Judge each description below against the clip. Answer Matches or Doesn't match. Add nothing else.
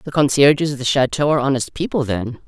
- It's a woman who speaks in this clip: Matches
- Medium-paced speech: Doesn't match